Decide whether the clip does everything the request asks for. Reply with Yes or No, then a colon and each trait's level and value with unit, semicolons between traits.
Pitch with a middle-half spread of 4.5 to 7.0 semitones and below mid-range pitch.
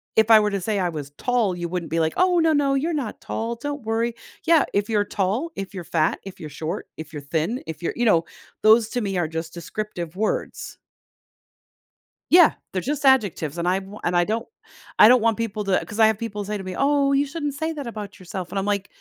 No: wide, 5.6 semitones; high, 210 Hz